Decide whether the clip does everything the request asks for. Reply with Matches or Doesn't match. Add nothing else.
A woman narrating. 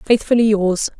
Matches